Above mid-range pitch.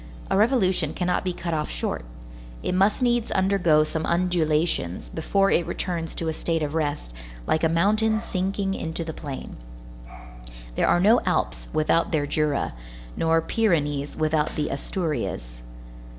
No: medium, 165 Hz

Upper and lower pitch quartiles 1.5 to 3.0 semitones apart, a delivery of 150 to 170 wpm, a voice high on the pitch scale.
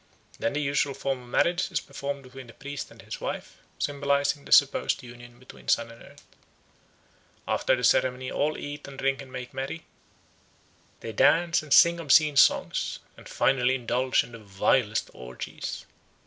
No: narrow, 2.6 semitones; average, 165 wpm; low, 135 Hz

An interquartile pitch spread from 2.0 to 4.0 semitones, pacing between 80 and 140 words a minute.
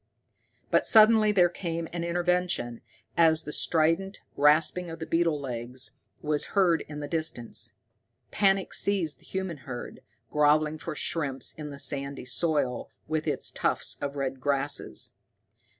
Yes: average, 3.5 semitones; slow, 135 wpm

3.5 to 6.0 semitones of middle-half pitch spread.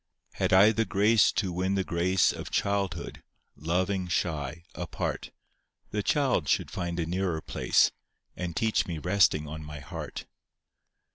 No: average, 2.9 semitones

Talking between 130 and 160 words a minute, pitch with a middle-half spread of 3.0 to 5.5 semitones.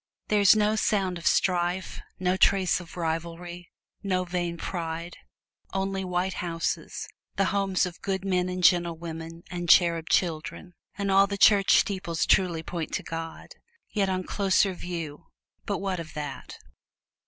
No: average, 155 wpm; narrow, 2.4 semitones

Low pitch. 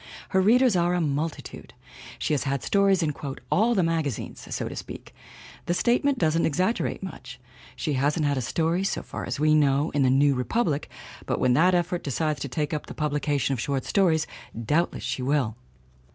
No: medium, 155 Hz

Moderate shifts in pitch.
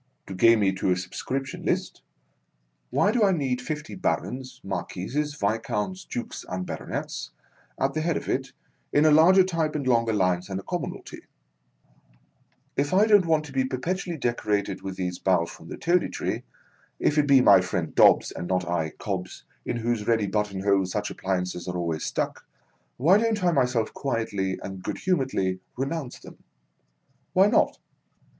No: wide, 8.2 semitones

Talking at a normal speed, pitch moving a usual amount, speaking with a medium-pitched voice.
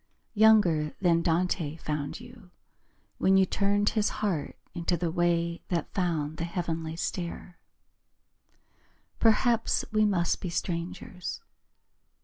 No: slow, 115 wpm; average, 3.4 semitones; medium, 175 Hz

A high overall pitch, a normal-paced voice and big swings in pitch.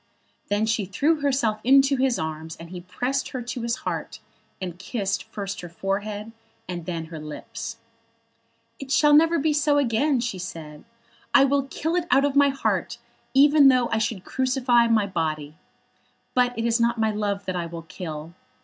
Yes: high, 225 Hz; average, 180 wpm; wide, 6.8 semitones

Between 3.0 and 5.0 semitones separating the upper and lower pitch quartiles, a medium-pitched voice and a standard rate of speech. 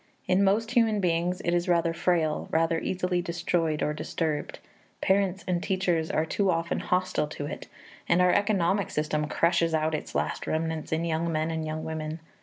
No: narrow, 2.4 semitones; medium, 170 Hz; average, 180 wpm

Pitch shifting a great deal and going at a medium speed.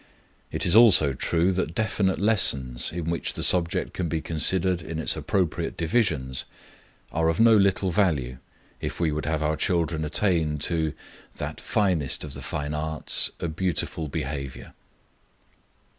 No: average, 3.5 semitones; average, 150 wpm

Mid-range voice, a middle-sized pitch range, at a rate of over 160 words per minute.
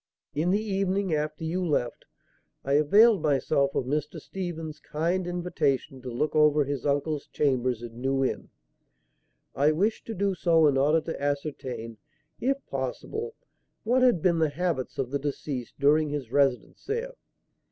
No: medium, 150 Hz; average, 4.5 semitones; average, 155 wpm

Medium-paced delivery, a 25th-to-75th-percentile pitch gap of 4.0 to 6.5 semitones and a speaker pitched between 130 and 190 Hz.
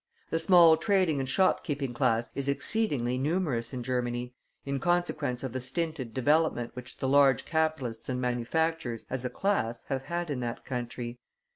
Yes: average, 160 wpm; average, 4.6 semitones; low, 135 Hz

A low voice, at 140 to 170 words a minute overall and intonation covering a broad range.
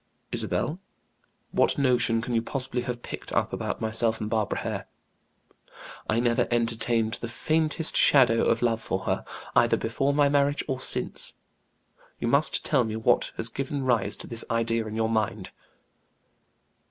No: low, 120 Hz; average, 155 wpm; average, 3.2 semitones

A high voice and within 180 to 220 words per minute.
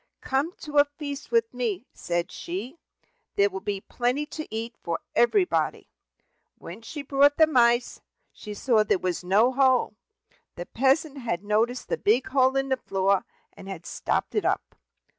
No: high, 240 Hz; average, 165 wpm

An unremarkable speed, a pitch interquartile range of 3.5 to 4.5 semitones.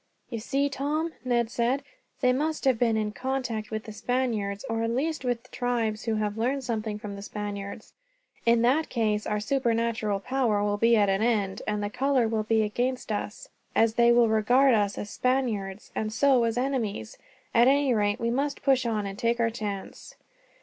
No: average, 190 wpm; average, 3.1 semitones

